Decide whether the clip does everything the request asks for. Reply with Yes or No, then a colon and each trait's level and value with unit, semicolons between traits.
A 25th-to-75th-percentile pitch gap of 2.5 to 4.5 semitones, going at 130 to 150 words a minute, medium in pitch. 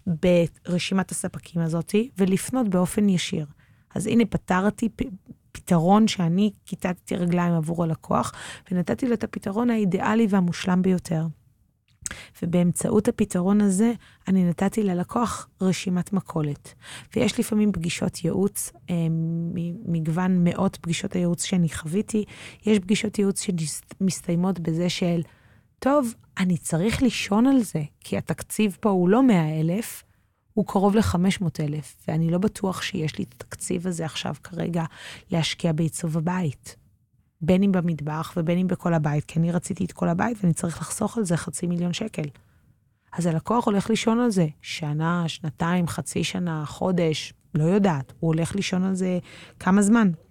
Yes: average, 3.5 semitones; average, 135 wpm; medium, 180 Hz